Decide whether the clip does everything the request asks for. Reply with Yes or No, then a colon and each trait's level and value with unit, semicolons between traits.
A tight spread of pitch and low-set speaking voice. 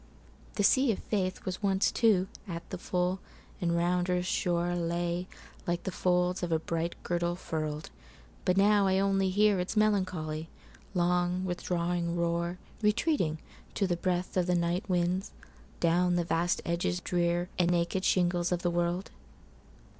No: narrow, 1.4 semitones; medium, 180 Hz